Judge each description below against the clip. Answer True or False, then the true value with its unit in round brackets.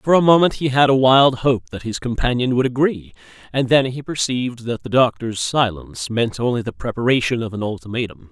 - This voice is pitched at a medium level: False (120 Hz)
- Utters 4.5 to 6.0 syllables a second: True (5.6 syllables/s)